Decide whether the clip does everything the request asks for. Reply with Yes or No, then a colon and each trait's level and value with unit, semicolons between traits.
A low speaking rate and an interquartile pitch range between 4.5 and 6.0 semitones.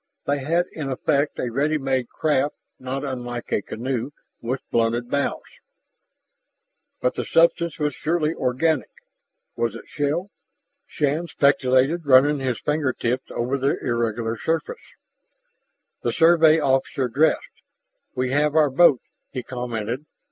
No: slow, 130 wpm; average, 3.5 semitones